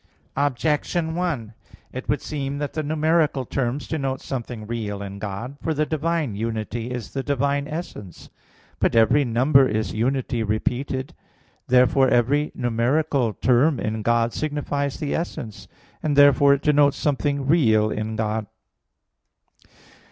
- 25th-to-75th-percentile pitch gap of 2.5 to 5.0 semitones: Yes, average, 4.2 semitones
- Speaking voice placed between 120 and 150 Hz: Yes, low, 135 Hz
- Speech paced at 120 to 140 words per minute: Yes, slow, 135 wpm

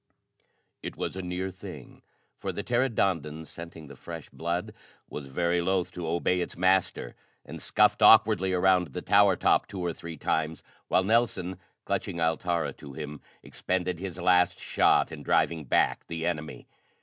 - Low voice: Yes, very low, 90 Hz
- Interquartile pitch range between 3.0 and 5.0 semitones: No, narrow, 2.4 semitones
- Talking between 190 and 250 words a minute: No, average, 160 wpm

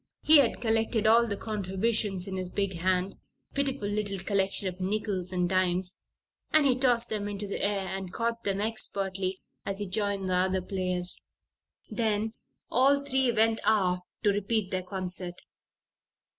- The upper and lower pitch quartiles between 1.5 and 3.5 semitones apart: Yes, average, 3.1 semitones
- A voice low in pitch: No, high, 200 Hz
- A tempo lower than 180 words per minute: Yes, average, 160 wpm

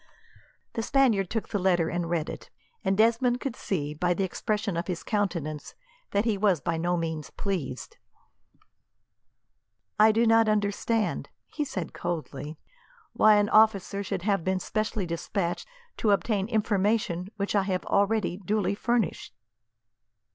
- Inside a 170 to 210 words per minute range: No, average, 145 wpm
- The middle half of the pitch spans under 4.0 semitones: Yes, average, 3.6 semitones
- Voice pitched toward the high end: Yes, high, 200 Hz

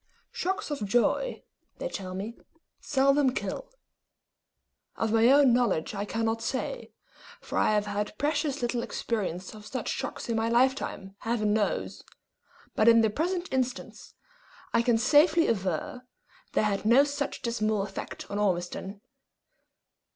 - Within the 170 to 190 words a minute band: No, average, 140 wpm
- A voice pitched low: No, high, 235 Hz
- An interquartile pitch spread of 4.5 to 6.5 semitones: Yes, average, 4.9 semitones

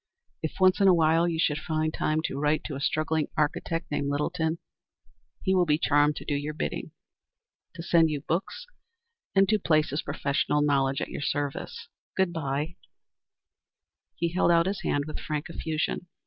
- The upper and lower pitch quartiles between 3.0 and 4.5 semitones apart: No, narrow, 2.5 semitones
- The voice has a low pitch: No, medium, 155 Hz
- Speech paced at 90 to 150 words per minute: No, average, 175 wpm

